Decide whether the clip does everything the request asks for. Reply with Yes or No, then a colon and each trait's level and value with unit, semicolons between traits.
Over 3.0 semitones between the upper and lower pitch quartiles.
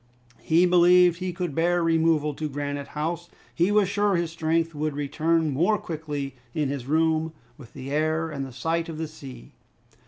No: narrow, 2.6 semitones